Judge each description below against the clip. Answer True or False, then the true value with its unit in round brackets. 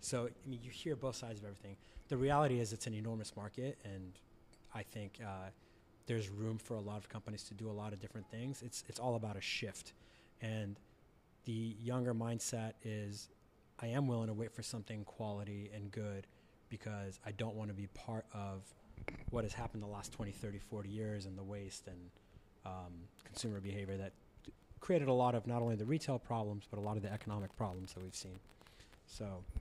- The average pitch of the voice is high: False (105 Hz)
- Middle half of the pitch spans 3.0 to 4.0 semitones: False (2.4 semitones)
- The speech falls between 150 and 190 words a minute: False (205 wpm)